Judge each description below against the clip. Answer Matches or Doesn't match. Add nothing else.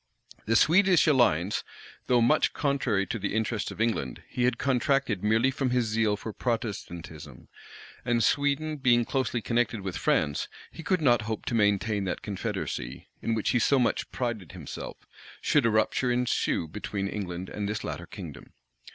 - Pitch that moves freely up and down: Doesn't match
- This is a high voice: Doesn't match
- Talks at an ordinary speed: Matches